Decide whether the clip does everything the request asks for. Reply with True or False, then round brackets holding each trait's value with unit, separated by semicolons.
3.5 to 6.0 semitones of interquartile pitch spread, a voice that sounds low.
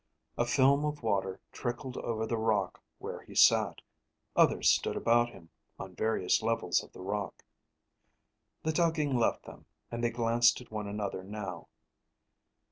False (3.1 semitones; 115 Hz)